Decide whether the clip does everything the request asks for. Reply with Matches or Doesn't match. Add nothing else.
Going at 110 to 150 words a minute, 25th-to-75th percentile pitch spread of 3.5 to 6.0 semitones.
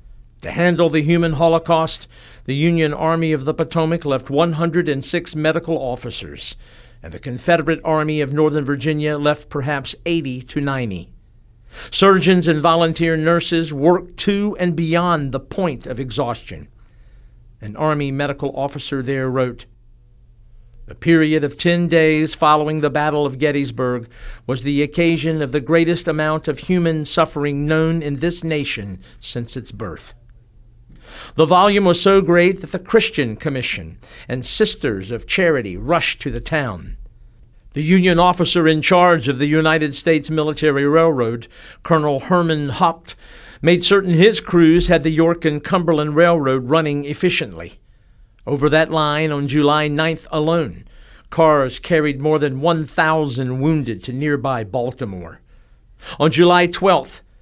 Matches